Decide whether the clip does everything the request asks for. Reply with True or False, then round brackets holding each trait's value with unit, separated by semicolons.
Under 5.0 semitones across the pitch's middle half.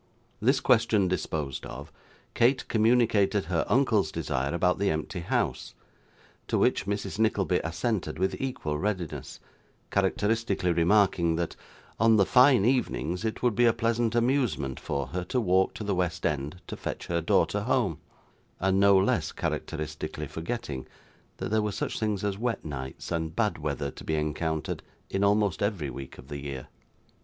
False (5.6 semitones)